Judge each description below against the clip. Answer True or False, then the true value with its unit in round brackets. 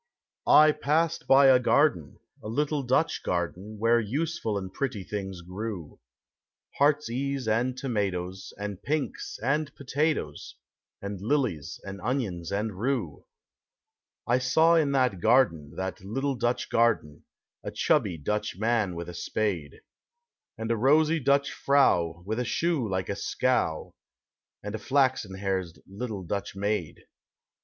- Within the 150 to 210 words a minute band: False (140 wpm)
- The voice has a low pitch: True (110 Hz)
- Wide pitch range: True (6.3 semitones)